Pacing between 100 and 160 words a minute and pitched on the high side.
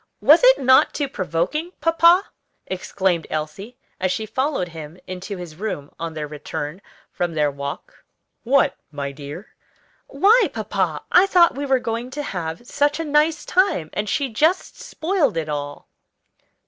Yes: average, 155 wpm; high, 205 Hz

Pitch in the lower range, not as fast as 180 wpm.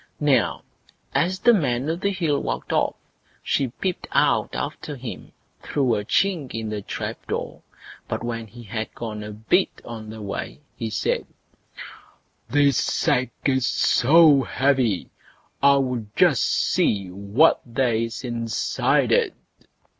Yes: low, 125 Hz; average, 140 wpm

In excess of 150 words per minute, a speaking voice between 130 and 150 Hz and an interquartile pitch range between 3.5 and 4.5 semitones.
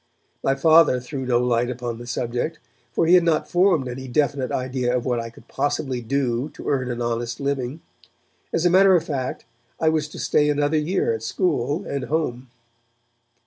Yes: average, 185 wpm; low, 135 Hz; average, 4.2 semitones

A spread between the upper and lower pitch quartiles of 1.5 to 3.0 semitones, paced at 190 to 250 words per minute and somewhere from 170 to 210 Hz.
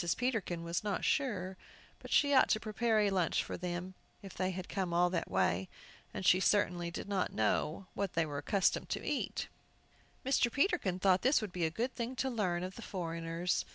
No: average, 3.9 semitones; average, 200 wpm; medium, 185 Hz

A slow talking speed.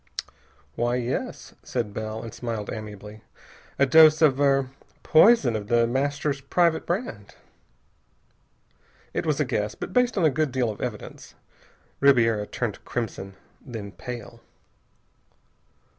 Yes: slow, 130 wpm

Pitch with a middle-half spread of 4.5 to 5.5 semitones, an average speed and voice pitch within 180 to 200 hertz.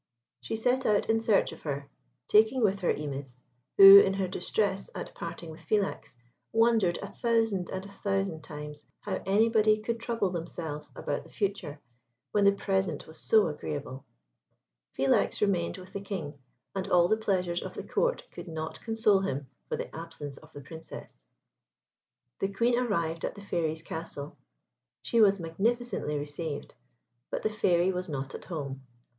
Yes: average, 5.1 semitones; average, 165 wpm; high, 190 Hz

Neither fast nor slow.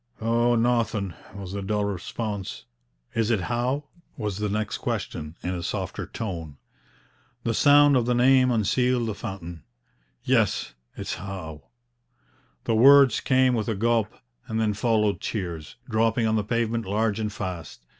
Yes: average, 150 wpm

